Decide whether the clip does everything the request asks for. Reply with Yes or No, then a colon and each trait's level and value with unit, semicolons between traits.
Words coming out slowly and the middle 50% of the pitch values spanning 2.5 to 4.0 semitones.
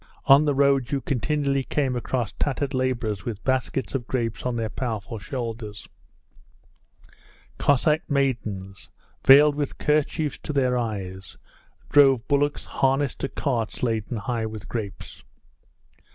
Yes: slow, 125 wpm; average, 3.7 semitones